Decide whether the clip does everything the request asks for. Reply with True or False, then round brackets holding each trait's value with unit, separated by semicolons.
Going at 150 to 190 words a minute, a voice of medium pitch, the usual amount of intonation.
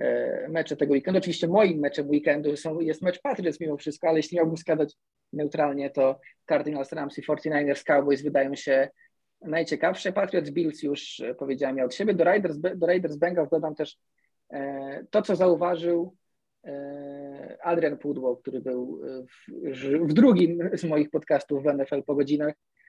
True (160 wpm; 150 Hz; 3.3 semitones)